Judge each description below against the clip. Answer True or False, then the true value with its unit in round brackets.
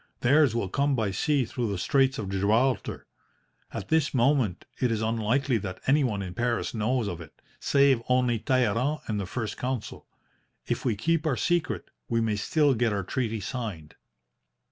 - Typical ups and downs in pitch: True (4.2 semitones)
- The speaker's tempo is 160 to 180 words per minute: True (170 wpm)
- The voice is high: False (120 Hz)